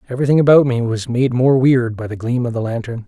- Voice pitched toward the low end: Yes, low, 125 Hz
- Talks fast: Yes, fast, 255 wpm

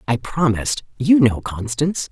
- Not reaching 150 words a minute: Yes, average, 140 wpm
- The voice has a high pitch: No, low, 135 Hz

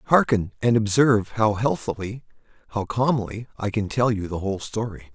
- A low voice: Yes, low, 110 Hz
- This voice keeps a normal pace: Yes, average, 150 wpm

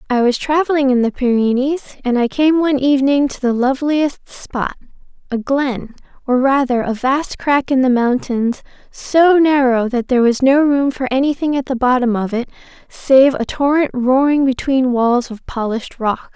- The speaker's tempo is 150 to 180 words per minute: Yes, average, 170 wpm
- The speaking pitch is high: Yes, very high, 265 Hz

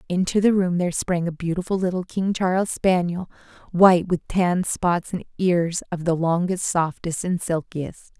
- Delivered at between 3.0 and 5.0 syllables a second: Yes, 4.7 syllables/s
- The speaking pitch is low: No, medium, 175 Hz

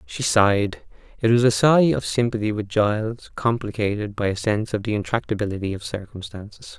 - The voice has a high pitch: No, low, 105 Hz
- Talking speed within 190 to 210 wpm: No, average, 170 wpm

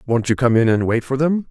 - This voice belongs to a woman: No, male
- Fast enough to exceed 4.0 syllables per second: Yes, 5.9 syllables/s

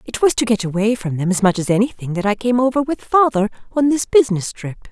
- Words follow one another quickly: Yes, fast, 255 wpm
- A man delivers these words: No, female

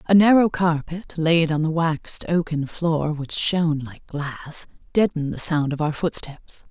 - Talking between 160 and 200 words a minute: Yes, average, 170 wpm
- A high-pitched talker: No, medium, 160 Hz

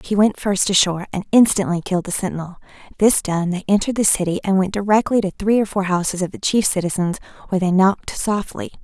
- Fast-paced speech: Yes, fast, 210 wpm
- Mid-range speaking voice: No, high, 195 Hz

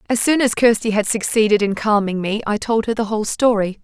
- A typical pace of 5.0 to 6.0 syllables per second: Yes, 5.9 syllables/s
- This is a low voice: No, high, 215 Hz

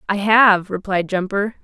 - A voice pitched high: Yes, high, 200 Hz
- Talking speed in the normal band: Yes, average, 145 wpm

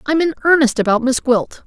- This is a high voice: Yes, very high, 265 Hz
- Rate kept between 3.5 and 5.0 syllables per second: No, 5.5 syllables/s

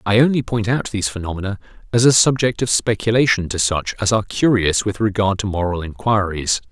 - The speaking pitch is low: Yes, low, 105 Hz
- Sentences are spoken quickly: No, average, 190 wpm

